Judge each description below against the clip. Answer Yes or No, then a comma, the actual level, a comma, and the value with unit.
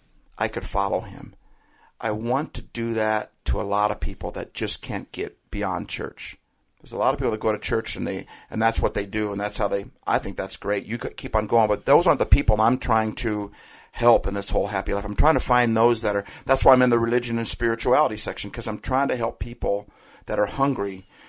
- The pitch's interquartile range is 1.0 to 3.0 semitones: Yes, average, 2.7 semitones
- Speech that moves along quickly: Yes, fast, 250 wpm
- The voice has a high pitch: No, low, 110 Hz